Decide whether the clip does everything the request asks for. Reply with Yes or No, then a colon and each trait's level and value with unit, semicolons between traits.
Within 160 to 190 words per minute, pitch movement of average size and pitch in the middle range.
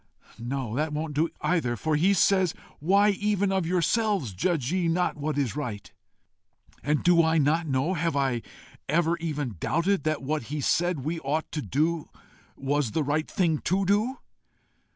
Yes: average, 170 wpm; average, 3.7 semitones; medium, 155 Hz